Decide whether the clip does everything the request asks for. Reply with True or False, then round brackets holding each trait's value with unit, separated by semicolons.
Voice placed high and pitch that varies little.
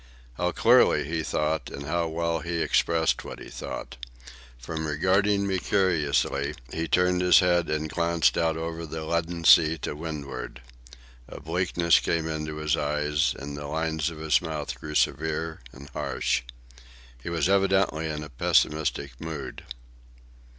False (80 Hz; 1.9 semitones)